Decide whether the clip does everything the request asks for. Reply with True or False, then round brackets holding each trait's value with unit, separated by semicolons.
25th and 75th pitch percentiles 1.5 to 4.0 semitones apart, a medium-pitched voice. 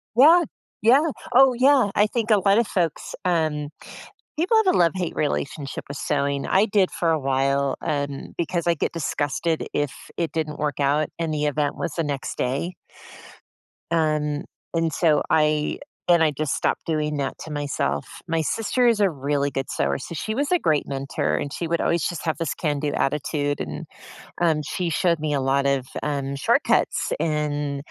True (3.4 semitones; 155 Hz)